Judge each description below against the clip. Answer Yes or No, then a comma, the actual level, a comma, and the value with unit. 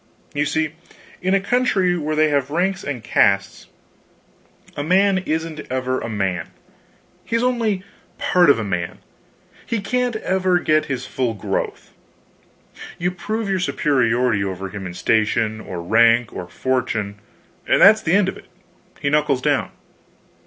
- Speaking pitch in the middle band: Yes, medium, 145 Hz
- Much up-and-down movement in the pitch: Yes, wide, 8.8 semitones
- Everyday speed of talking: Yes, average, 150 wpm